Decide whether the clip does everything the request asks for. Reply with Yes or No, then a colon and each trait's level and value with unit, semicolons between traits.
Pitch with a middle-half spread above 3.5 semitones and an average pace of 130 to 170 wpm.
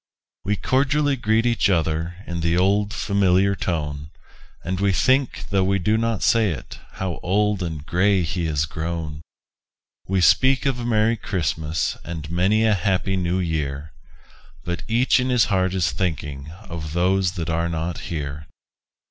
Yes: average, 4.3 semitones; average, 160 wpm